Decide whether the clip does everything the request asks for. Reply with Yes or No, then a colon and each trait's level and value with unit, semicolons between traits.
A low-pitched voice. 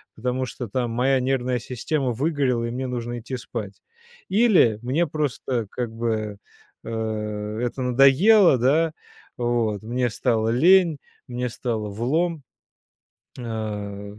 Yes: low, 125 Hz